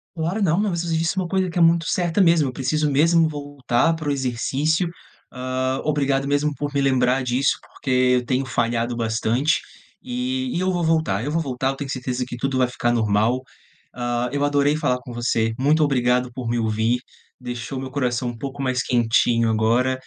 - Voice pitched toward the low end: Yes, low, 130 Hz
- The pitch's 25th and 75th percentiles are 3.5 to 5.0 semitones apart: Yes, average, 4.1 semitones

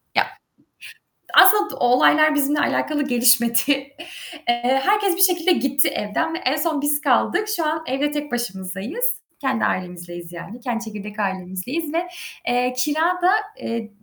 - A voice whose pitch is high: Yes, very high, 270 Hz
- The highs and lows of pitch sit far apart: Yes, wide, 5.7 semitones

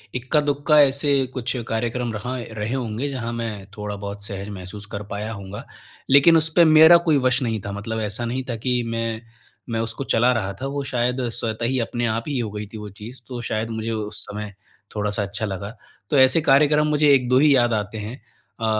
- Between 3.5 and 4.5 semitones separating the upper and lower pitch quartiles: Yes, average, 3.8 semitones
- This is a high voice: No, low, 115 Hz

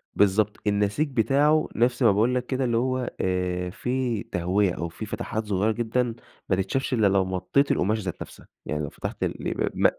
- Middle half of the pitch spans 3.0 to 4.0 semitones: No, average, 4.9 semitones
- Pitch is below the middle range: Yes, low, 110 Hz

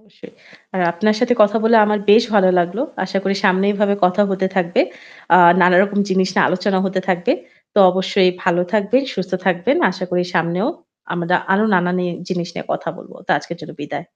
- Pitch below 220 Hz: Yes, high, 190 Hz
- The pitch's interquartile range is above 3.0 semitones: No, narrow, 2.4 semitones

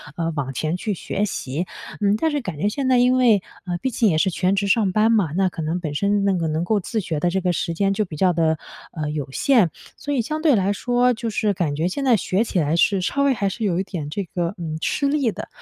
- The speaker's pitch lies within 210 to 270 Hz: No, high, 195 Hz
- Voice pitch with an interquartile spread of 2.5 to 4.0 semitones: No, average, 5.0 semitones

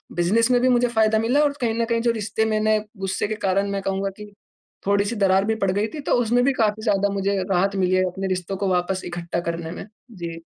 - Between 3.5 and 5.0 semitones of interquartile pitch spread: No, average, 2.8 semitones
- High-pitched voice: Yes, high, 200 Hz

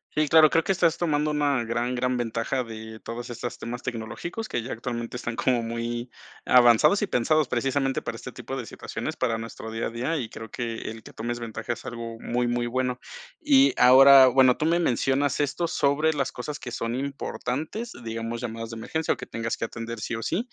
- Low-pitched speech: Yes, low, 125 Hz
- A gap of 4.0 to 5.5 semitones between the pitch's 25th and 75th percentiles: No, average, 3.5 semitones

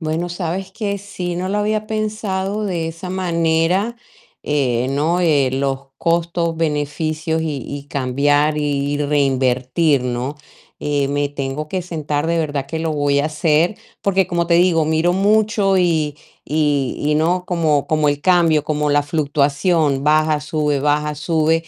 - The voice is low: No, medium, 155 Hz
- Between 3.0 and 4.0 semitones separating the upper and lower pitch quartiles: Yes, average, 3.4 semitones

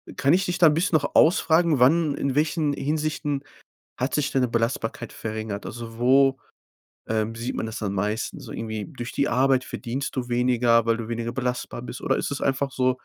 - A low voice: Yes, low, 130 Hz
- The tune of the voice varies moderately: Yes, average, 3.7 semitones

